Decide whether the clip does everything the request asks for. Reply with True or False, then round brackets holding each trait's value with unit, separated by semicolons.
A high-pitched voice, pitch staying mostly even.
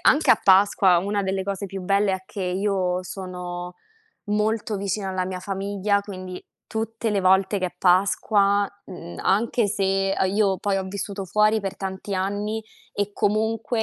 True (195 Hz; 1.6 semitones)